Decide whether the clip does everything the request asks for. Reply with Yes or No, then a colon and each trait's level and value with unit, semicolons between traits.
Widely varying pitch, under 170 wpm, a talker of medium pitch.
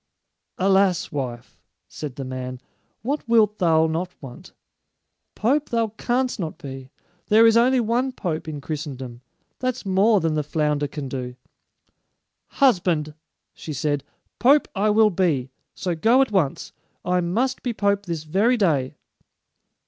Yes: wide, 7.1 semitones; average, 140 wpm; medium, 180 Hz